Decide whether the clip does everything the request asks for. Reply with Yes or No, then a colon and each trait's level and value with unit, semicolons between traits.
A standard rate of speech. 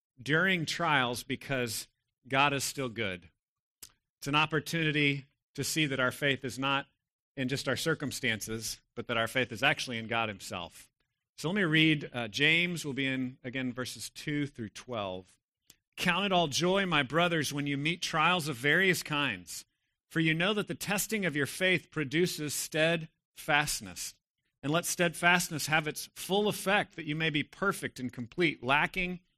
Yes: average, 170 wpm